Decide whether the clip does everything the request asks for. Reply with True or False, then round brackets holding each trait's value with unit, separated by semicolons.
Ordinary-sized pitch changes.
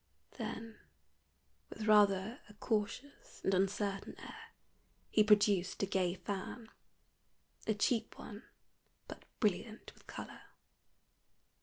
False (2.1 semitones)